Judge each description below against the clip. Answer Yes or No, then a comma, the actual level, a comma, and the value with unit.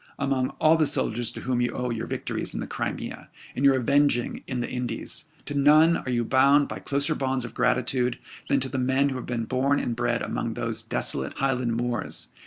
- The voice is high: No, low, 130 Hz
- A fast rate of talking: Yes, fast, 210 wpm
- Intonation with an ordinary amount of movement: No, narrow, 2.3 semitones